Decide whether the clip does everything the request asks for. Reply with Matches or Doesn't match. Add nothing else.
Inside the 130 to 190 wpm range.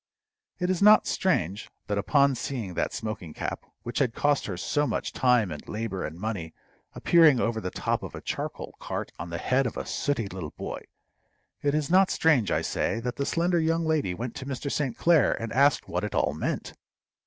Doesn't match